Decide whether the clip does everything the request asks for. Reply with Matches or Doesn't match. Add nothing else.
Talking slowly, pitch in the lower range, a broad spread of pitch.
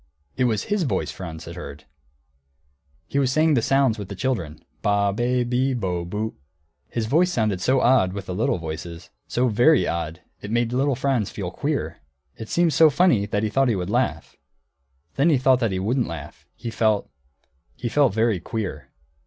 Doesn't match